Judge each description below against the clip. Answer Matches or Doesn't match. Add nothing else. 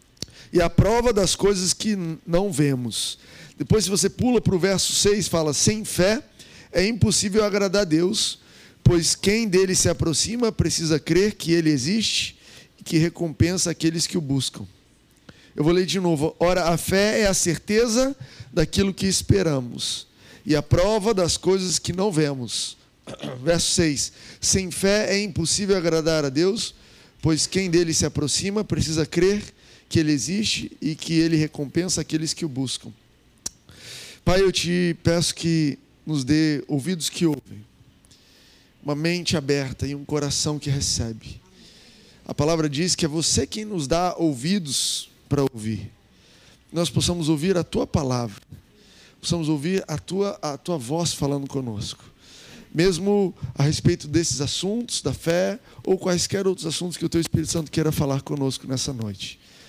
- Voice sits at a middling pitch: Matches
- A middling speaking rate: Matches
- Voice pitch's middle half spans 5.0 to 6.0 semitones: Doesn't match